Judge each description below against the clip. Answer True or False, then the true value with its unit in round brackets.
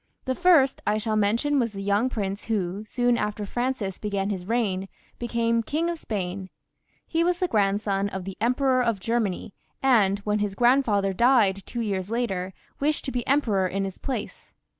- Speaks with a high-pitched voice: True (215 Hz)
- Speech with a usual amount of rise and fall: True (4.1 semitones)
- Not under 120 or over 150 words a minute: False (180 wpm)